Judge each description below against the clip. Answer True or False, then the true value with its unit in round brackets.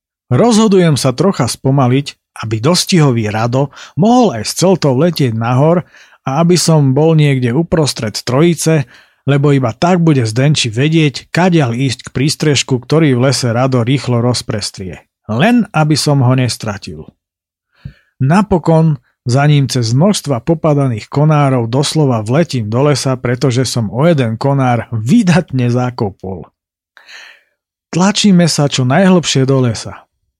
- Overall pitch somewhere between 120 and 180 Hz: True (140 Hz)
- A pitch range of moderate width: True (4.5 semitones)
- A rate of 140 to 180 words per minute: False (130 wpm)